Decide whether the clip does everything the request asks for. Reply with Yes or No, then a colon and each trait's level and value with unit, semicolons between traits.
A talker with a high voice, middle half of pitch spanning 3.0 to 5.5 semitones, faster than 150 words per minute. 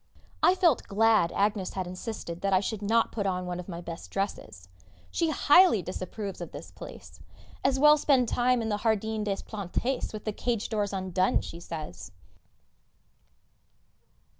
Yes: high, 205 Hz; average, 4.0 semitones; average, 165 wpm